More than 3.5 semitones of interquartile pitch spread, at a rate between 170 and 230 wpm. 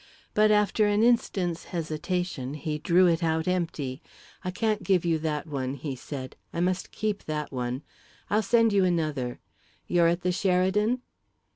No: average, 4.5 semitones; average, 160 wpm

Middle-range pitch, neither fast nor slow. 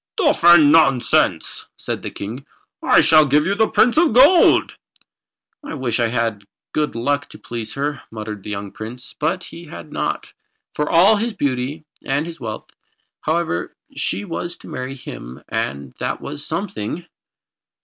Yes: medium, 145 Hz; average, 170 wpm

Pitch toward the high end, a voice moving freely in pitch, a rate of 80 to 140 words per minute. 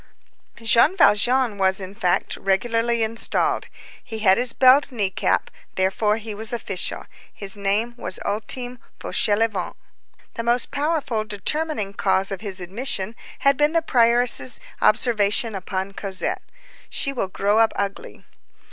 No: high, 220 Hz; average, 3.7 semitones; slow, 135 wpm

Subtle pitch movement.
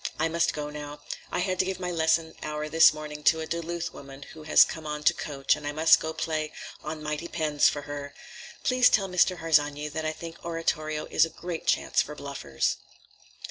Yes: narrow, 1.7 semitones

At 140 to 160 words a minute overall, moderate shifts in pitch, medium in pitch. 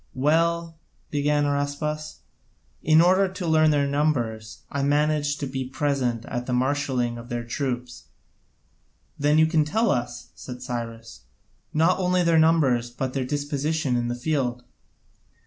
Yes: average, 145 wpm; average, 4.0 semitones; medium, 145 Hz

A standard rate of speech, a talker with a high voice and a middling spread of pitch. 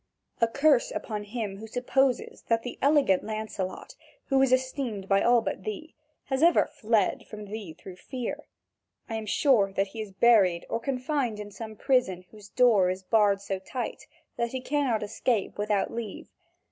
Yes: average, 170 wpm; high, 220 Hz; average, 4.0 semitones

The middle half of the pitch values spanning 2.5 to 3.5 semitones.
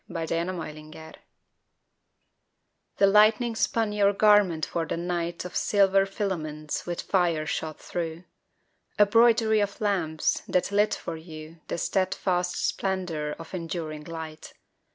No: average, 4.0 semitones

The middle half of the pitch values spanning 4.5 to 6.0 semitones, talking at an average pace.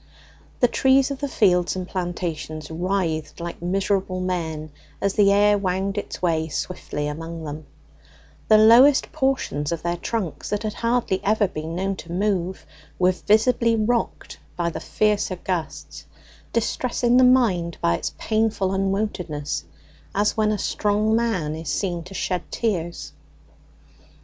No: average, 4.1 semitones; average, 145 wpm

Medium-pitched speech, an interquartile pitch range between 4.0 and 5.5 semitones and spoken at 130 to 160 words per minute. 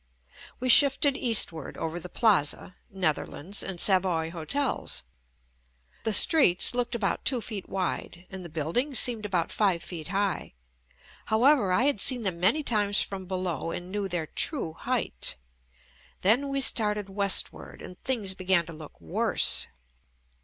No: high, 195 Hz; average, 5.1 semitones; average, 145 wpm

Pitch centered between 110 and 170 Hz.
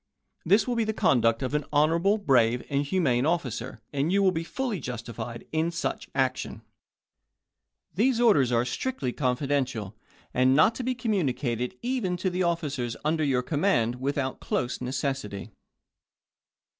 Yes: medium, 140 Hz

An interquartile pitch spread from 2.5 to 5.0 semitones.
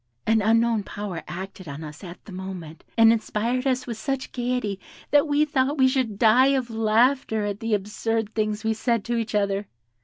Yes: average, 3.6 semitones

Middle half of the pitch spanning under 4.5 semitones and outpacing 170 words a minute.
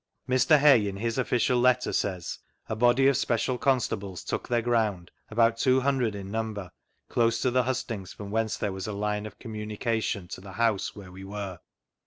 Yes: average, 3.5 semitones; average, 200 wpm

